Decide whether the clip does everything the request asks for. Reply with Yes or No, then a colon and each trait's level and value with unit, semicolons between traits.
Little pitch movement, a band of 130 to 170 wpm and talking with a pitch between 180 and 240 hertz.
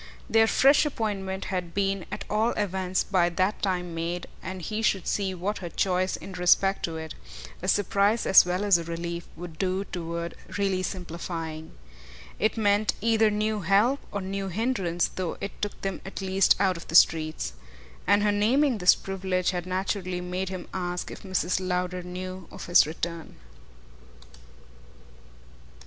Yes: narrow, 2.3 semitones; average, 160 wpm; medium, 185 Hz